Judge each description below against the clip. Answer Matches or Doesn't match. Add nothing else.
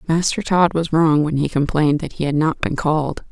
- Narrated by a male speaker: Doesn't match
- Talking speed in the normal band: Doesn't match